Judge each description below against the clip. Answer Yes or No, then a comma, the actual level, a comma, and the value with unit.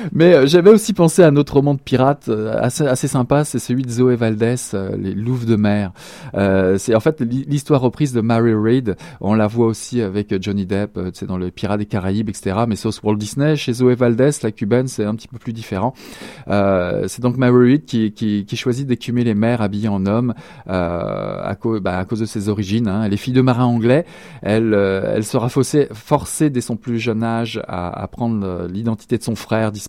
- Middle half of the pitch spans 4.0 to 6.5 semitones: No, average, 3.6 semitones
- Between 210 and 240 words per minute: Yes, fast, 220 wpm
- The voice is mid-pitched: No, low, 115 Hz